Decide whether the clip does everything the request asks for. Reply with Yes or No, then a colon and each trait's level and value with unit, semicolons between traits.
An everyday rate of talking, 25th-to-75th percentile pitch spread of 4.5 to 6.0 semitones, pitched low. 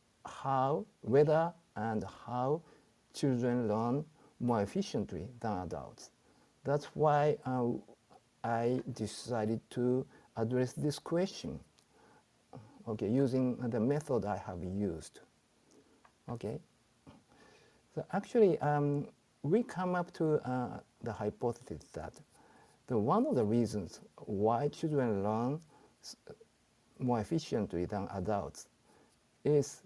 No: slow, 105 wpm; average, 5.1 semitones; low, 125 Hz